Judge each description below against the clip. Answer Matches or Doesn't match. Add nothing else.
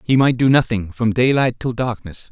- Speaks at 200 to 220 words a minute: Matches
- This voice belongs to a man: Matches